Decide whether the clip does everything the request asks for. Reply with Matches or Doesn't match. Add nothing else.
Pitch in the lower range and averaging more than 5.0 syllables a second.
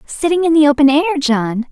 Doesn't match